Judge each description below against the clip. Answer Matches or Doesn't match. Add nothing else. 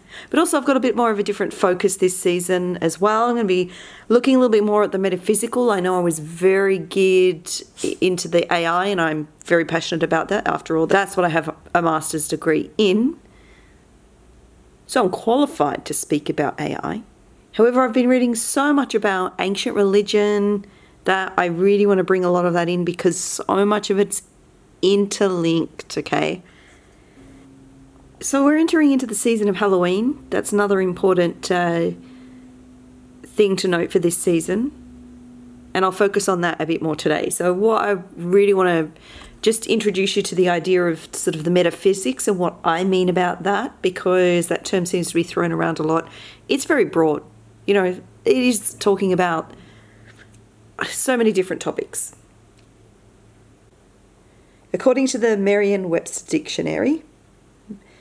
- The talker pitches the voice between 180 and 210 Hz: Matches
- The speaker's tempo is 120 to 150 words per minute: Doesn't match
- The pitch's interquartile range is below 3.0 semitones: Doesn't match